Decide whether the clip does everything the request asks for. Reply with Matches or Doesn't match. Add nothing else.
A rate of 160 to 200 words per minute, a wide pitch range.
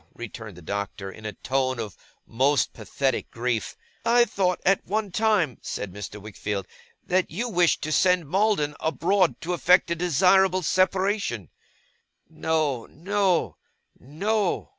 Doesn't match